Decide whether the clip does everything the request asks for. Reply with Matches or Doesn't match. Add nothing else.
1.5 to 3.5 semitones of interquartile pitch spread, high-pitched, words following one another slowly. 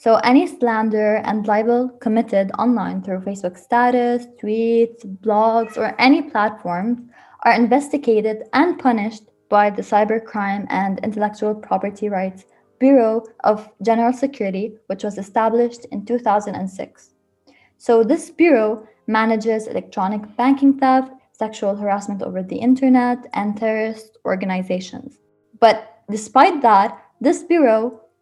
Matches